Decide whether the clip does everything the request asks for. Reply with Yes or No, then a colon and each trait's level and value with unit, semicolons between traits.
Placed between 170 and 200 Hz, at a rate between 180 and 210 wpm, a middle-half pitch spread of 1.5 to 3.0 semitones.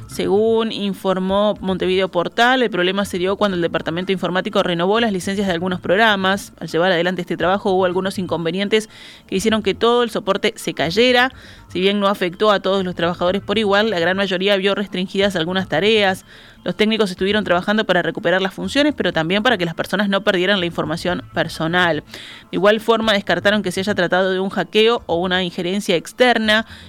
Yes: high, 190 Hz; fast, 190 wpm; narrow, 2.6 semitones